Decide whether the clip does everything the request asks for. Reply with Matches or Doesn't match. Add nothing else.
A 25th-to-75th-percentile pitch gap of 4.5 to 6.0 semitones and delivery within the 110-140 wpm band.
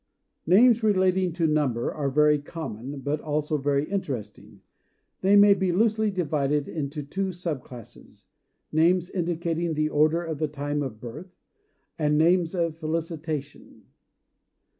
Doesn't match